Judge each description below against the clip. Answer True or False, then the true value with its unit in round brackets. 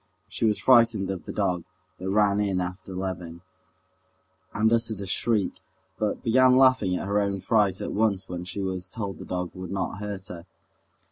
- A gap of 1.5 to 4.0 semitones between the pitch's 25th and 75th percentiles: True (2.7 semitones)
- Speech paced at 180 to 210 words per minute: True (185 wpm)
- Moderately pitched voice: False (100 Hz)